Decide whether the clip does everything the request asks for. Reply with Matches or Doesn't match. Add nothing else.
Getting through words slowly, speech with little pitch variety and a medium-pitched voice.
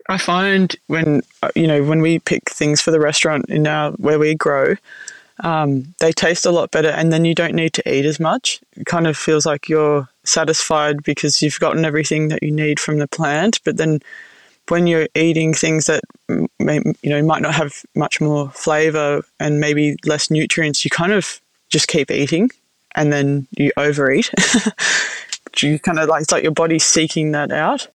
Doesn't match